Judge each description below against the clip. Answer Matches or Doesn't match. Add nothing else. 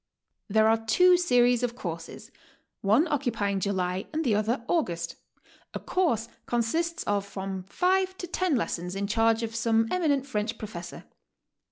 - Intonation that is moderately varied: Doesn't match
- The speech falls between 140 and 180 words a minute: Matches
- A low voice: Doesn't match